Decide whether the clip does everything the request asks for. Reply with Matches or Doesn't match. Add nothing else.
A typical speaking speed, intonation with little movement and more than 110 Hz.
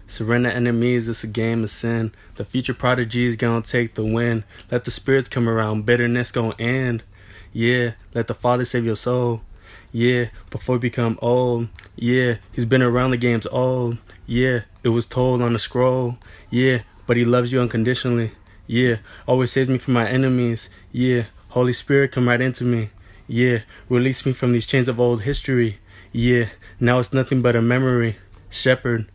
Matches